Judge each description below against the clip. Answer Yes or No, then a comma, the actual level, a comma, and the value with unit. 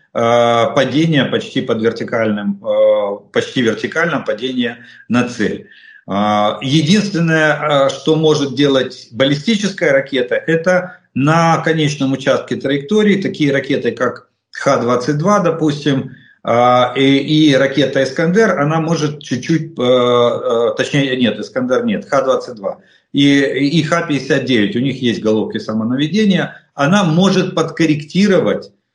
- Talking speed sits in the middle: No, slow, 100 wpm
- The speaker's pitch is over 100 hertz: Yes, medium, 140 Hz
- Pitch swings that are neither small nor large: Yes, average, 4.6 semitones